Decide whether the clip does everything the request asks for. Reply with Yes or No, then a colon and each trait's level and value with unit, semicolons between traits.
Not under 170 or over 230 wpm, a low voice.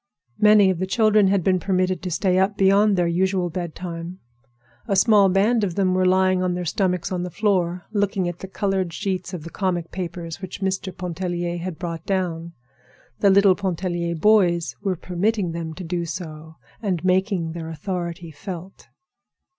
No: average, 175 wpm; medium, 185 Hz